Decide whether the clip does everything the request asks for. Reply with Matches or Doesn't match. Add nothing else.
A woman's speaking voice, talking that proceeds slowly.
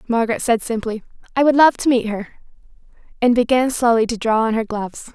Doesn't match